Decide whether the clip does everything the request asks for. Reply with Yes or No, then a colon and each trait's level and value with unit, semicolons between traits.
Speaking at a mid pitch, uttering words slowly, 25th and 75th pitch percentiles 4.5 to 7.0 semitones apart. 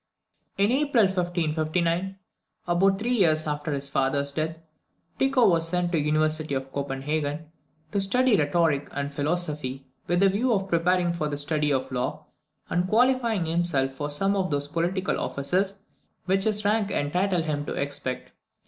No: medium, 165 Hz; average, 160 wpm; average, 4.9 semitones